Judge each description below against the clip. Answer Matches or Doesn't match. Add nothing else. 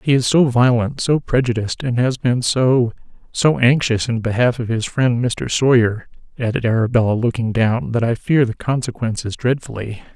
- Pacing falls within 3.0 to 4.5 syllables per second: Doesn't match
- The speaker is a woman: Doesn't match